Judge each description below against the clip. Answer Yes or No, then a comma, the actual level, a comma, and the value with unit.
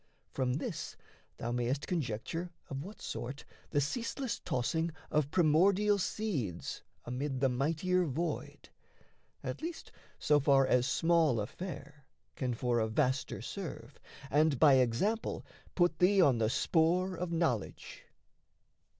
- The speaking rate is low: Yes, slow, 125 wpm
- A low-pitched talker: No, medium, 150 Hz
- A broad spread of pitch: Yes, wide, 5.9 semitones